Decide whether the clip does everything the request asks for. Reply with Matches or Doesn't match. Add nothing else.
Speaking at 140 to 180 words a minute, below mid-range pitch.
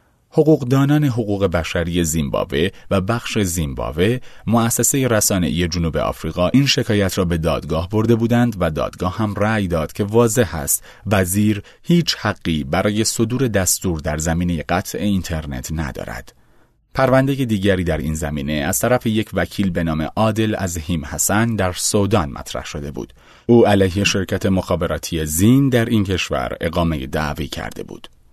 Matches